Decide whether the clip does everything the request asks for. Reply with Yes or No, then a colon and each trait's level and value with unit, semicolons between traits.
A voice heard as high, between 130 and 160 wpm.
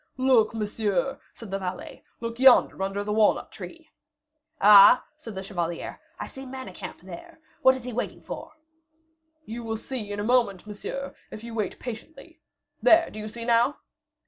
No: high, 225 Hz; average, 170 wpm